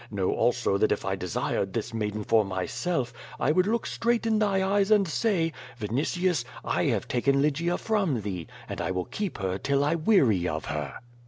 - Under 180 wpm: No, average, 190 wpm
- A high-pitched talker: No, low, 135 Hz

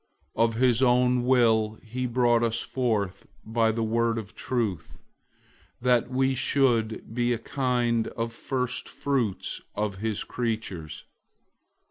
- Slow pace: Yes, slow, 130 wpm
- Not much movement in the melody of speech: Yes, narrow, 2.1 semitones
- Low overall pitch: Yes, low, 115 Hz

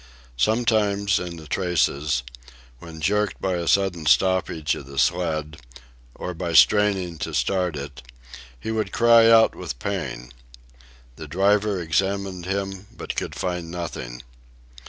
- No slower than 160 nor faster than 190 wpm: No, slow, 135 wpm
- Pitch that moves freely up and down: No, average, 3.9 semitones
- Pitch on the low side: Yes, very low, 90 Hz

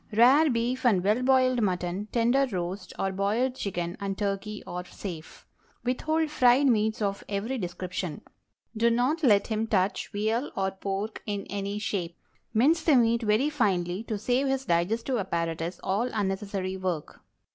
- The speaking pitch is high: Yes, high, 210 Hz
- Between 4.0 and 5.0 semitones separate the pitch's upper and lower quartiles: Yes, average, 4.4 semitones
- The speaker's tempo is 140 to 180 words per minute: Yes, average, 155 wpm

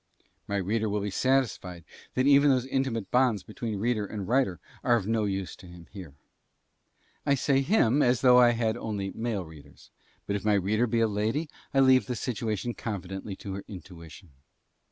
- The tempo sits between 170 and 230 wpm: Yes, average, 185 wpm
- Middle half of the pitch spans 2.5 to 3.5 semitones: No, average, 4.3 semitones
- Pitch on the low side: Yes, low, 110 Hz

